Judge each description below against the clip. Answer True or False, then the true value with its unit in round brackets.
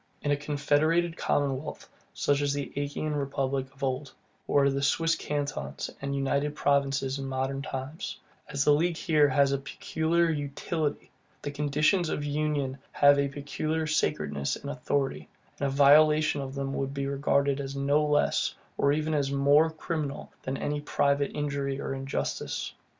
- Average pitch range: False (1.4 semitones)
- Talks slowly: False (160 wpm)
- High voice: False (140 Hz)